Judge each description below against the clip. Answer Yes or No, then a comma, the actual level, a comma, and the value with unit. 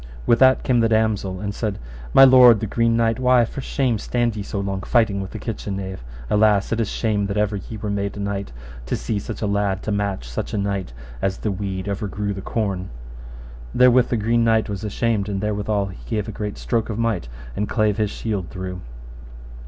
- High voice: No, low, 105 Hz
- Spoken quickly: Yes, fast, 215 wpm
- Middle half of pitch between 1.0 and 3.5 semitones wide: Yes, narrow, 2.5 semitones